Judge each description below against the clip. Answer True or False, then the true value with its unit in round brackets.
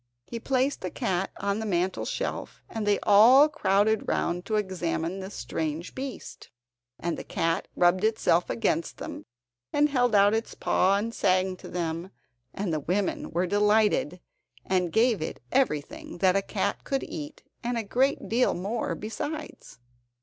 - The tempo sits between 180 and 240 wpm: False (160 wpm)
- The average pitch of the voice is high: True (200 Hz)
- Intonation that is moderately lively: True (4.4 semitones)